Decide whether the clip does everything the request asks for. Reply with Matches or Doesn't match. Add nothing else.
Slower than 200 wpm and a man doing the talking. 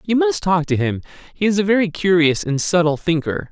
Doesn't match